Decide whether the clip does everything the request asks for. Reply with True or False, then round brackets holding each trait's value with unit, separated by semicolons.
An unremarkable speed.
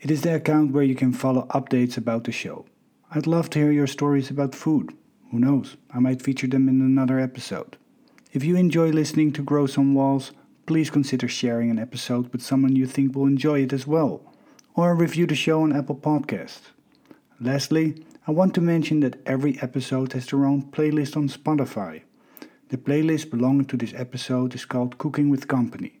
True (190 wpm)